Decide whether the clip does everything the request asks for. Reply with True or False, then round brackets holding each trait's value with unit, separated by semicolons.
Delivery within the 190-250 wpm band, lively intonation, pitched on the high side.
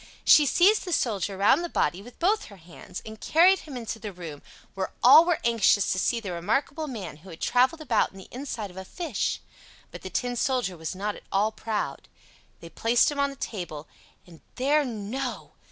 True (200 wpm; 6.5 semitones; 225 Hz)